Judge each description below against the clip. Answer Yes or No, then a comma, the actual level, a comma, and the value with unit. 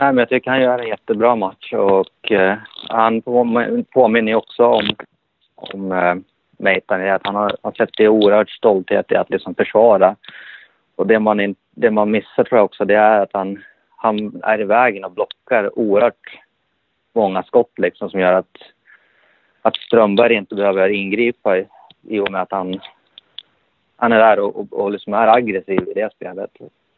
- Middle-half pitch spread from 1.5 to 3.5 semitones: Yes, average, 3.0 semitones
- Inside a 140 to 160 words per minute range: No, average, 170 wpm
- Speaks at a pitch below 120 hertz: Yes, low, 105 Hz